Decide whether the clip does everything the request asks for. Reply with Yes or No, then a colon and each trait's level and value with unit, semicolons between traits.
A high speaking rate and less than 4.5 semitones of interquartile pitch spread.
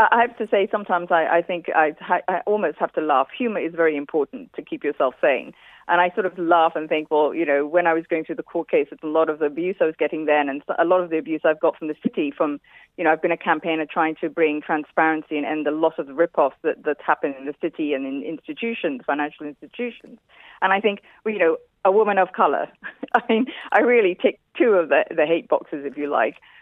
No: fast, 255 wpm; wide, 5.5 semitones